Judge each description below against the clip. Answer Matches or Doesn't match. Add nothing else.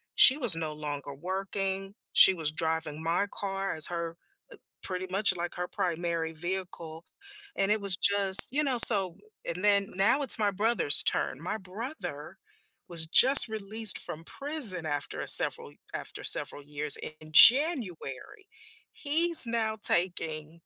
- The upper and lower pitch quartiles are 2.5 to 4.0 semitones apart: Doesn't match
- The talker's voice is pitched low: Doesn't match